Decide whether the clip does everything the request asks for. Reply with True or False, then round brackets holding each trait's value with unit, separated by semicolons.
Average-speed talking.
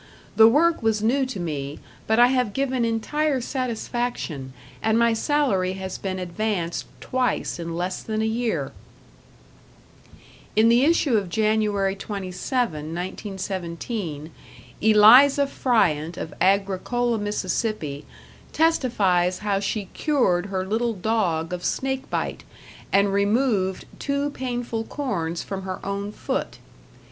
False (120 wpm)